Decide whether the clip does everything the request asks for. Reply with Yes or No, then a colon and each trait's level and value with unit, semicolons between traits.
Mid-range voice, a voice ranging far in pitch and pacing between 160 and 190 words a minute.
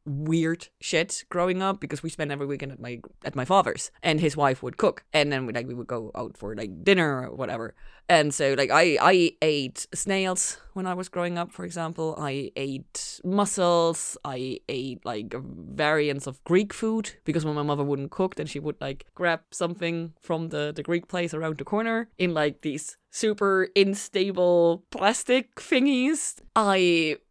No: medium, 165 Hz; average, 4.2 semitones; average, 185 wpm